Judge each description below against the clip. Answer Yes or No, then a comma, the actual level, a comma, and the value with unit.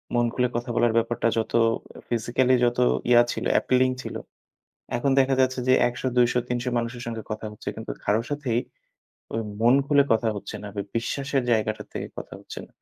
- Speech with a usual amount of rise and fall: No, narrow, 2.0 semitones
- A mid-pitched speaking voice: No, low, 120 Hz